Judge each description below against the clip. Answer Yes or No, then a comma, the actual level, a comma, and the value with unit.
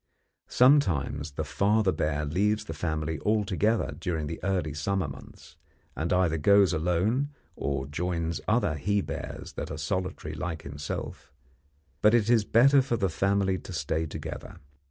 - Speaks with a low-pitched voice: Yes, very low, 90 Hz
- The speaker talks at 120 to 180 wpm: Yes, average, 150 wpm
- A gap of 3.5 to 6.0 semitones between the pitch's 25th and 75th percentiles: Yes, average, 5.1 semitones